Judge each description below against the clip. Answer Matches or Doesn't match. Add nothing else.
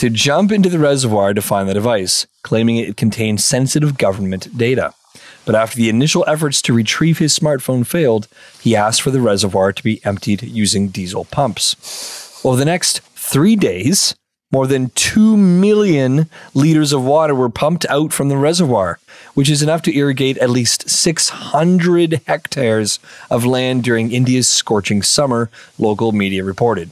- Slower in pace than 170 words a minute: Matches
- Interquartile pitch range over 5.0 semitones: Matches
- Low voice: Matches